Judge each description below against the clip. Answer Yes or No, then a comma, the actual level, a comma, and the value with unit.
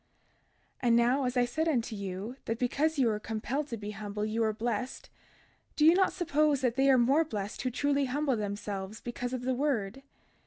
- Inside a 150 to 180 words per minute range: No, fast, 205 wpm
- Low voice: No, high, 245 Hz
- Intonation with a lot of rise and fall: No, average, 4.5 semitones